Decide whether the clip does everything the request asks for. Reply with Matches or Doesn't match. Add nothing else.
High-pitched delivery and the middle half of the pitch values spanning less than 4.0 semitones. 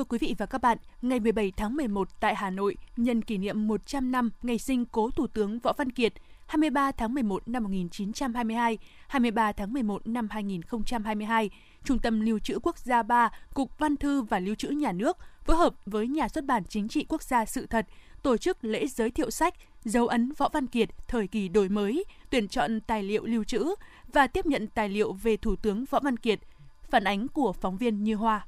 Matches